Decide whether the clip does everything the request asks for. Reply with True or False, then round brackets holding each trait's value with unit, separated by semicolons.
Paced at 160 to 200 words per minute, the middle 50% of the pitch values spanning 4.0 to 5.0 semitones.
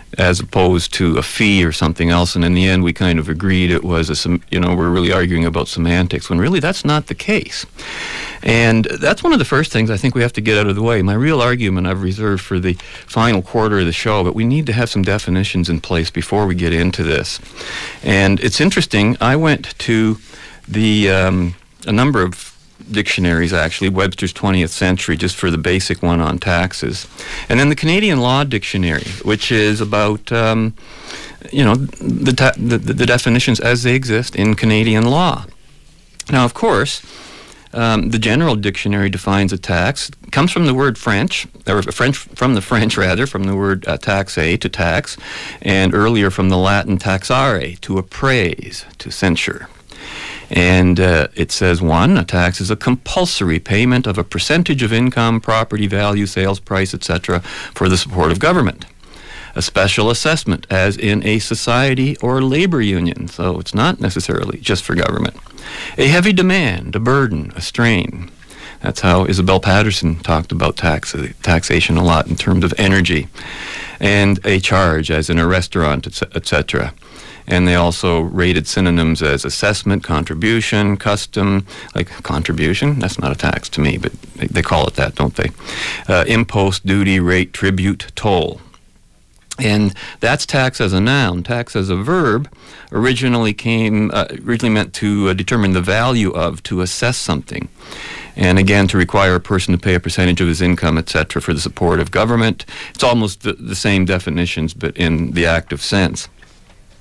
True (180 wpm; 4.3 semitones)